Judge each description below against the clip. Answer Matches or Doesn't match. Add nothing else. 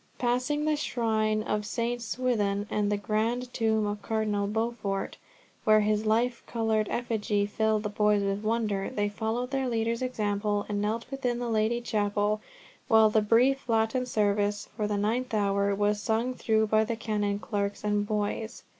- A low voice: Doesn't match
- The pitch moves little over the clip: Matches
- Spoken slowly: Doesn't match